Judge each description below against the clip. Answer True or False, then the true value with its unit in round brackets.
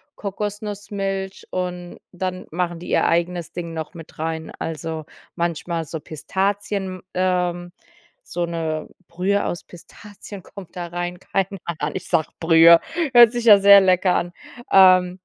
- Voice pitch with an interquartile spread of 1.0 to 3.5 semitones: True (2.4 semitones)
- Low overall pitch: False (180 Hz)